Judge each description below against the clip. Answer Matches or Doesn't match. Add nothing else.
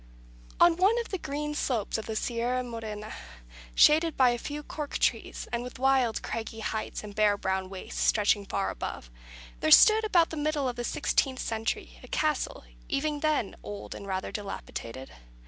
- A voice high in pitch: Matches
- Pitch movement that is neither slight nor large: Doesn't match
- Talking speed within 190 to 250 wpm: Doesn't match